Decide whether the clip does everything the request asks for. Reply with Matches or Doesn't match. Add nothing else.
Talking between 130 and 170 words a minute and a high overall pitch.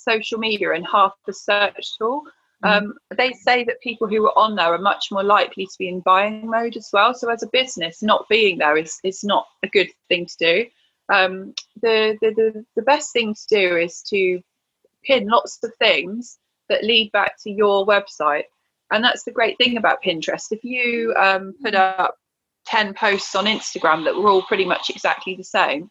Doesn't match